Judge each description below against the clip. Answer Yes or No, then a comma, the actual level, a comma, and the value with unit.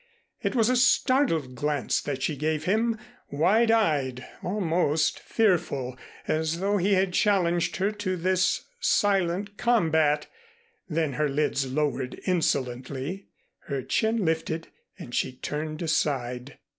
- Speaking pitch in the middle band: Yes, medium, 160 Hz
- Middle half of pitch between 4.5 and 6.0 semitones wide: Yes, wide, 5.6 semitones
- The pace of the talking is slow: Yes, slow, 125 wpm